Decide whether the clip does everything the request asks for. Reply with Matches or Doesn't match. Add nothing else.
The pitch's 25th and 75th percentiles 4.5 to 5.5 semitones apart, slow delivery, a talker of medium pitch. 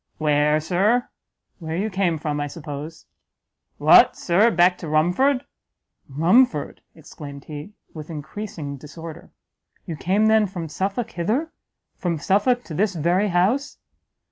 Matches